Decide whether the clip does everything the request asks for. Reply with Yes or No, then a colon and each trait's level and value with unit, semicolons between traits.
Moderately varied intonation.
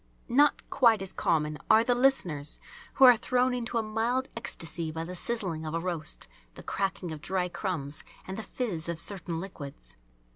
No: wide, 6.3 semitones